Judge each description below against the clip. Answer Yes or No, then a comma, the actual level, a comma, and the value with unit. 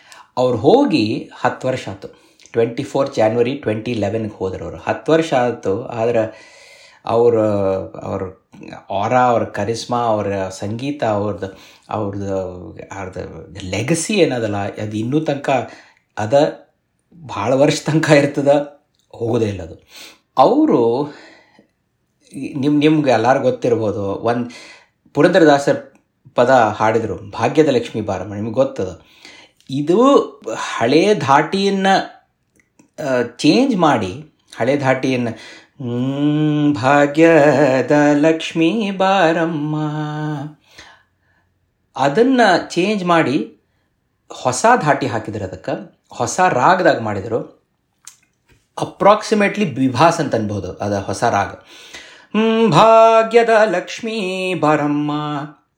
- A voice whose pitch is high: No, medium, 140 Hz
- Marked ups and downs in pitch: Yes, wide, 6.2 semitones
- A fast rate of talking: No, average, 90 wpm